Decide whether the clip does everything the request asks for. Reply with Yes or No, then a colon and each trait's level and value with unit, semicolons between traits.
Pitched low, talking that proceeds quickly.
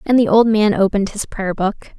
No: high, 210 Hz; fast, 240 wpm